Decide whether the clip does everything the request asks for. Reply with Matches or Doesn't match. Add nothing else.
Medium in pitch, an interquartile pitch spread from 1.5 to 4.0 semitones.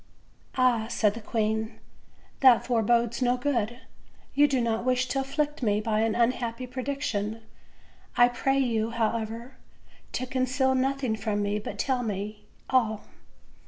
Doesn't match